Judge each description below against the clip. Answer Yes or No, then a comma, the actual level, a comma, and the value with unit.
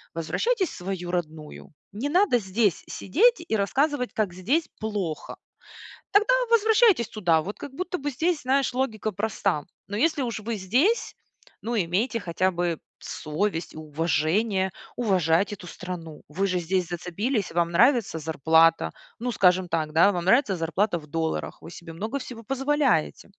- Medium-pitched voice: No, high, 195 Hz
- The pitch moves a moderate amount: No, wide, 6.7 semitones